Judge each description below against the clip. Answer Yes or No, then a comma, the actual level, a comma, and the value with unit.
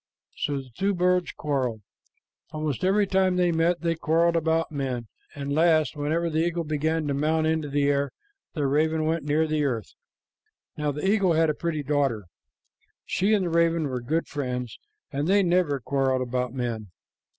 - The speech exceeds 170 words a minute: Yes, average, 180 wpm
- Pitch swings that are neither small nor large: Yes, average, 3.2 semitones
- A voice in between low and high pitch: Yes, medium, 155 Hz